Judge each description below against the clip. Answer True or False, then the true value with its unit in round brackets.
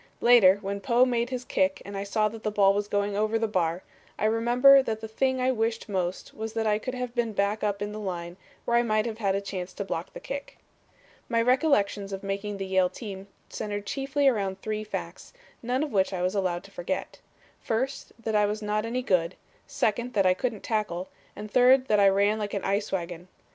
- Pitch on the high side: True (210 Hz)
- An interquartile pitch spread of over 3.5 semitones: False (3.2 semitones)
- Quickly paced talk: True (220 wpm)